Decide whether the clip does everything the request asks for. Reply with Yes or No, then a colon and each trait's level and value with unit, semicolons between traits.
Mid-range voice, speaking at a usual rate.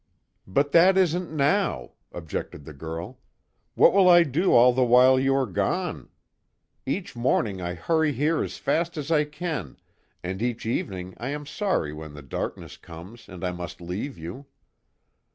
No: low, 125 Hz; average, 165 wpm